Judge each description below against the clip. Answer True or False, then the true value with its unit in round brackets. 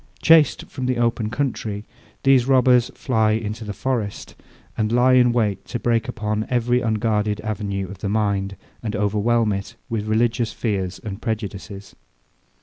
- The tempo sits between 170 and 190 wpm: False (155 wpm)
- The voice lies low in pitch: True (110 Hz)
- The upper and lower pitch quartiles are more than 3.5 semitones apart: False (2.7 semitones)